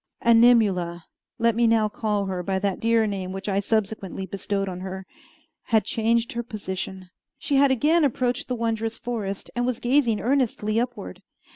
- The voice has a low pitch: No, high, 220 Hz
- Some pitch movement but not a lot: Yes, average, 3.5 semitones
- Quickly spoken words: No, average, 165 wpm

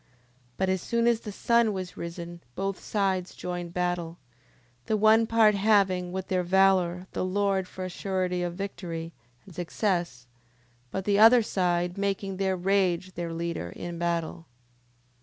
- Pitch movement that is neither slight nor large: No, narrow, 2.3 semitones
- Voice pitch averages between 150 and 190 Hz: Yes, medium, 185 Hz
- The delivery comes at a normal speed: Yes, average, 160 wpm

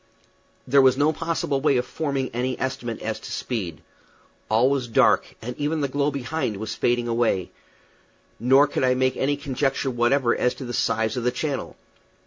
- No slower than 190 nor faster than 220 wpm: No, average, 180 wpm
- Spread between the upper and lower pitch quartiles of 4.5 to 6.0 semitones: No, average, 2.7 semitones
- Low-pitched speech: Yes, low, 130 Hz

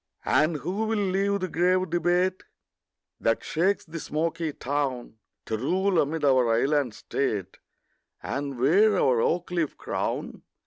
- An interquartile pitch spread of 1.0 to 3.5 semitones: No, average, 5.2 semitones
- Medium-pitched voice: Yes, medium, 160 Hz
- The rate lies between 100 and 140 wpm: Yes, slow, 135 wpm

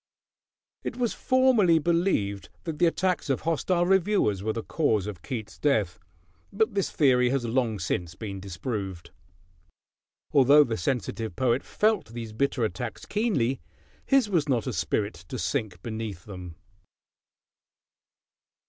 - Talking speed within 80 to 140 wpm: Yes, slow, 135 wpm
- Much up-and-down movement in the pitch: Yes, wide, 8.2 semitones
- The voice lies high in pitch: No, low, 125 Hz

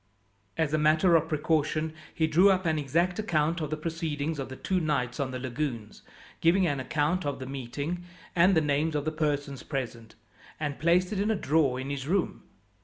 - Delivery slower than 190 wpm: No, average, 200 wpm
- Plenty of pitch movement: No, average, 3.0 semitones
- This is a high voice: No, medium, 155 Hz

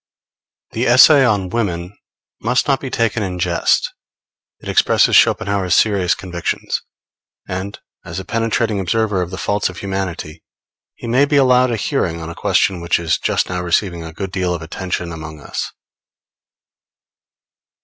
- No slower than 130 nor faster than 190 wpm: Yes, average, 155 wpm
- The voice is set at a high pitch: No, very low, 95 Hz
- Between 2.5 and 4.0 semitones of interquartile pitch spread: No, average, 4.5 semitones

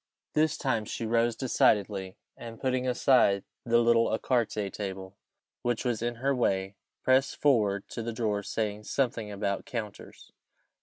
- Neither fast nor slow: Yes, average, 145 wpm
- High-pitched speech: No, low, 115 Hz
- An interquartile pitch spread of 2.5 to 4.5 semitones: Yes, average, 3.4 semitones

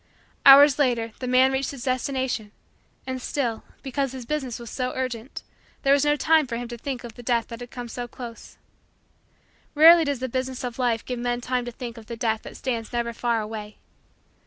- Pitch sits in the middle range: No, very high, 250 Hz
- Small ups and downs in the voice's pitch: Yes, narrow, 2.2 semitones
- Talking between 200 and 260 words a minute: Yes, fast, 205 wpm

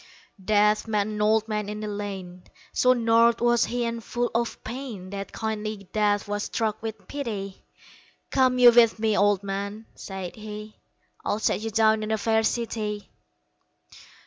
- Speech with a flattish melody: Yes, narrow, 1.9 semitones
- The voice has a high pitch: Yes, high, 215 Hz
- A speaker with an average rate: Yes, average, 165 wpm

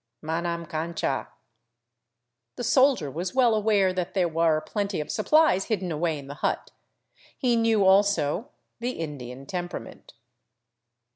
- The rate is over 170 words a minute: No, average, 140 wpm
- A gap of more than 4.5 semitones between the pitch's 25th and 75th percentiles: Yes, average, 5.3 semitones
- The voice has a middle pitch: Yes, medium, 180 Hz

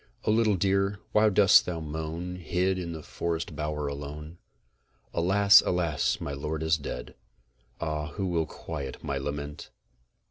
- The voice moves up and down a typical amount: Yes, average, 3.7 semitones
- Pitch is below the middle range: Yes, very low, 80 Hz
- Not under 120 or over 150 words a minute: Yes, average, 145 wpm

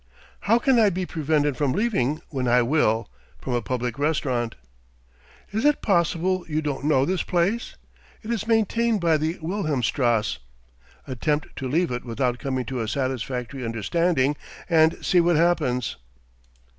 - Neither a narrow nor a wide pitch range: No, wide, 5.8 semitones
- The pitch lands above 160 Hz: No, medium, 150 Hz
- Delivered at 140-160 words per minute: Yes, average, 150 wpm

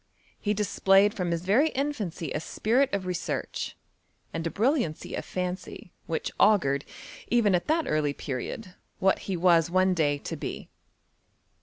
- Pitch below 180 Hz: No, medium, 185 Hz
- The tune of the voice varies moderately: Yes, average, 4.3 semitones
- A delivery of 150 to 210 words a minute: No, slow, 135 wpm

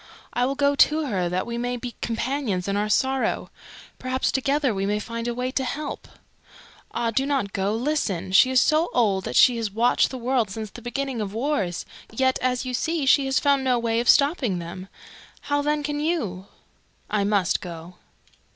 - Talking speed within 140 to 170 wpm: No, average, 195 wpm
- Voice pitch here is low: No, high, 245 Hz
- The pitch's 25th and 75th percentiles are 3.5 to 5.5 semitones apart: Yes, average, 5.1 semitones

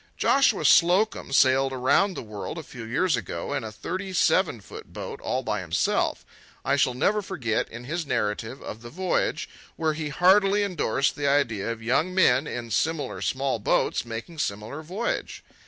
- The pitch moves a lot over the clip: Yes, wide, 7.3 semitones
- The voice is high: No, medium, 140 Hz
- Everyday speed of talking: Yes, average, 170 wpm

